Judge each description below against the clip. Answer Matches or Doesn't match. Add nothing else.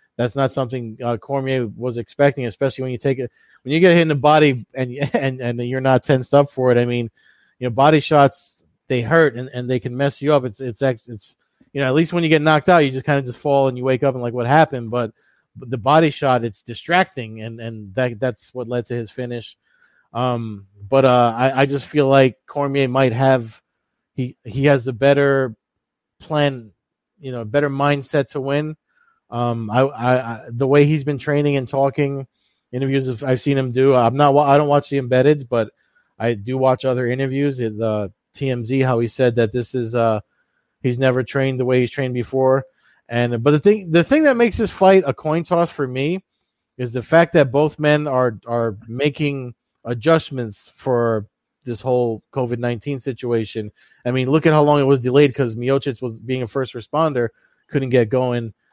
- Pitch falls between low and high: Doesn't match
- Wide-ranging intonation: Doesn't match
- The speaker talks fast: Matches